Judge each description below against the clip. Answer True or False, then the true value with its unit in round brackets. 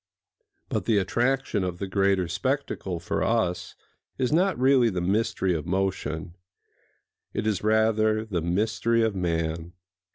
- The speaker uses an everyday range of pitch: True (4.3 semitones)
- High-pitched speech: False (100 Hz)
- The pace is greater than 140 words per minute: False (135 wpm)